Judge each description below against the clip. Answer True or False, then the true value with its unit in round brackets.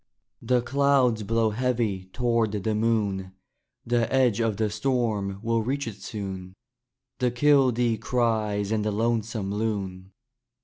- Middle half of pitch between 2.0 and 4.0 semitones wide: True (2.9 semitones)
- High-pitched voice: False (110 Hz)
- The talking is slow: True (130 wpm)